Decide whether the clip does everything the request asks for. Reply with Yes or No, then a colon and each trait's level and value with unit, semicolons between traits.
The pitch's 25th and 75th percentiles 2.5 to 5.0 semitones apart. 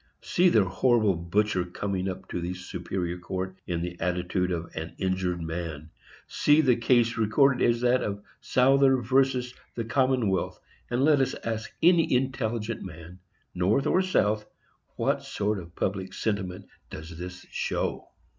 No: wide, 5.6 semitones